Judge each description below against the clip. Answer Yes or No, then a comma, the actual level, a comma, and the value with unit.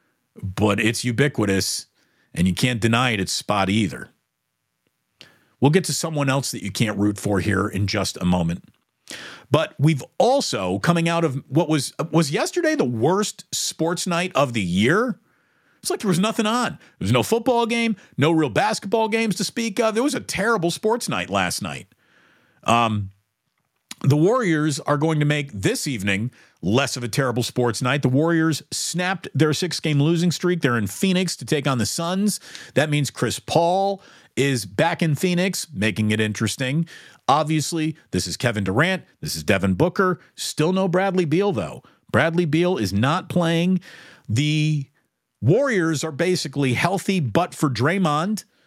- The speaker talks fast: No, average, 170 wpm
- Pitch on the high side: No, medium, 155 Hz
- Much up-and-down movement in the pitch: Yes, wide, 7.1 semitones